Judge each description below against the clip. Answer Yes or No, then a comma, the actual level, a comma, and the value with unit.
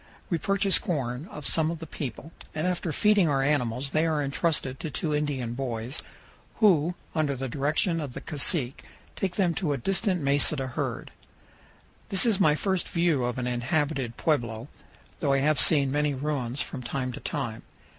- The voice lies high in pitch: No, medium, 145 Hz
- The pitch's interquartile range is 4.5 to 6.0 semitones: No, average, 4.0 semitones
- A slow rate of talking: No, average, 180 wpm